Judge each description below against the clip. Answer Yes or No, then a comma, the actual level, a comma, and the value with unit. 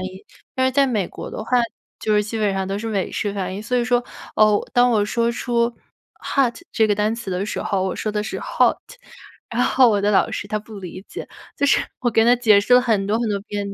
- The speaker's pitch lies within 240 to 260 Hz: No, high, 215 Hz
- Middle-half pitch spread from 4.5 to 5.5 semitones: No, average, 2.9 semitones